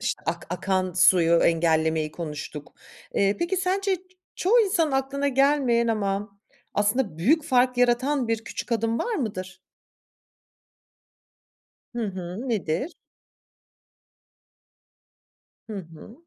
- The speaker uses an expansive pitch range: Yes, wide, 7.0 semitones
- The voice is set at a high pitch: Yes, high, 225 Hz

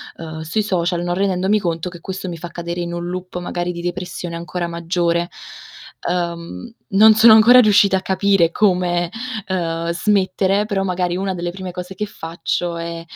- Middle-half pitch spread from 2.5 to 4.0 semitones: No, narrow, 2.1 semitones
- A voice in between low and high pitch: Yes, medium, 180 Hz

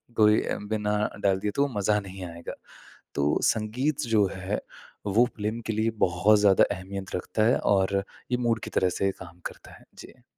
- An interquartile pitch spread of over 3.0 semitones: No, narrow, 2.4 semitones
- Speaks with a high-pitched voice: No, low, 105 Hz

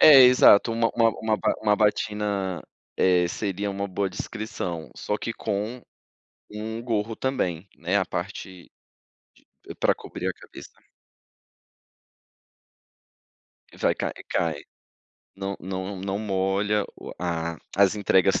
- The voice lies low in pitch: Yes, low, 100 Hz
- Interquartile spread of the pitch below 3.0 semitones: Yes, narrow, 2.5 semitones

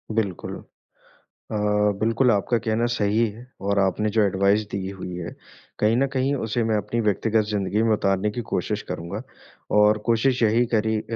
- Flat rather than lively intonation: Yes, narrow, 2.3 semitones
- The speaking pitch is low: Yes, low, 110 Hz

